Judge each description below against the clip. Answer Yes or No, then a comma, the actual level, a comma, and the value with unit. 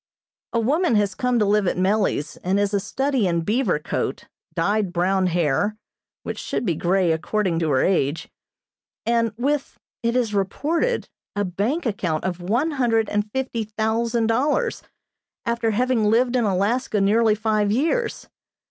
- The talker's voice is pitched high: Yes, high, 215 Hz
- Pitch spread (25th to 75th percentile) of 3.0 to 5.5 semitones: Yes, average, 4.1 semitones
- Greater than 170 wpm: No, average, 155 wpm